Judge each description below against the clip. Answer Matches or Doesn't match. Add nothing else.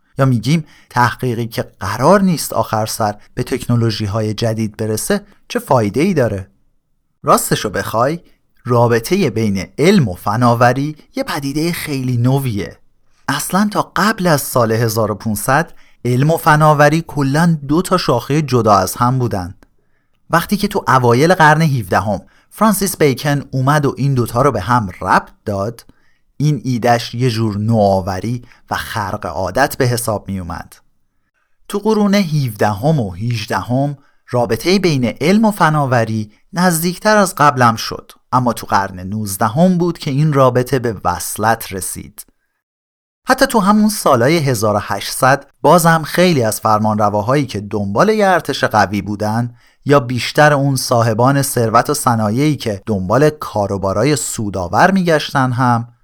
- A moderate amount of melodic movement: Doesn't match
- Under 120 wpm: Doesn't match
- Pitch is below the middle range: Matches